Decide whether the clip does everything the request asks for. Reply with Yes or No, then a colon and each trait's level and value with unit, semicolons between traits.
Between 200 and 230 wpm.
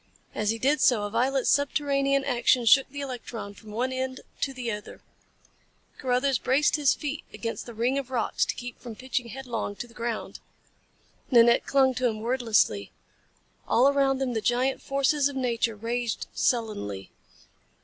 No: average, 165 wpm